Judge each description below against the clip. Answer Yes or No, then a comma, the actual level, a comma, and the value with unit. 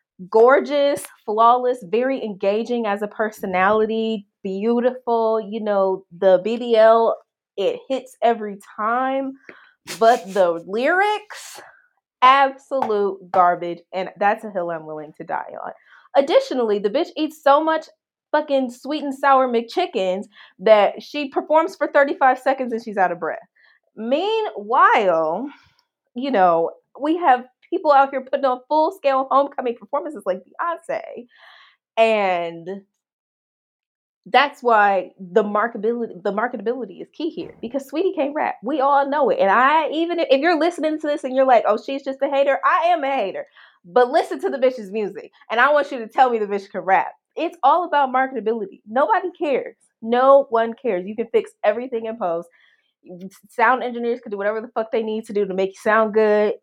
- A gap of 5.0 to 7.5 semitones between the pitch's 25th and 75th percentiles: Yes, wide, 5.5 semitones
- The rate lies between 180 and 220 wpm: No, average, 165 wpm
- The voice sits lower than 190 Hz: No, high, 240 Hz